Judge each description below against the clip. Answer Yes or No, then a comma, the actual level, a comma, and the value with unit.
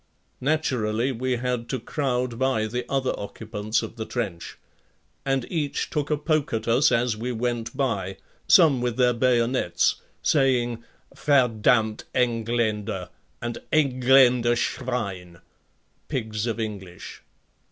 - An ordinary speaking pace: No, slow, 120 wpm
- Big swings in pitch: No, average, 2.9 semitones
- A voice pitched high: No, low, 120 Hz